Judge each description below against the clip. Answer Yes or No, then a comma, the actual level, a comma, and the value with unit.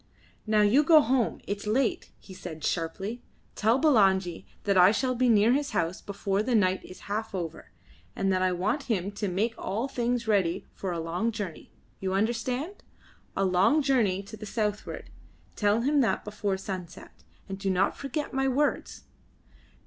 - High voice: Yes, high, 210 Hz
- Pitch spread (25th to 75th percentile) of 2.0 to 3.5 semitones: No, average, 4.3 semitones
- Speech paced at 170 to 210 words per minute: Yes, average, 175 wpm